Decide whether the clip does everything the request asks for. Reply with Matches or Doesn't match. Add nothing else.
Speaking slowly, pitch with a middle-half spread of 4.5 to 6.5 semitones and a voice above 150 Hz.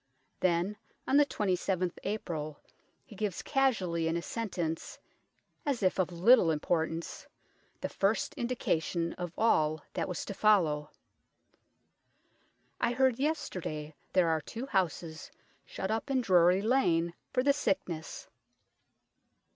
Matches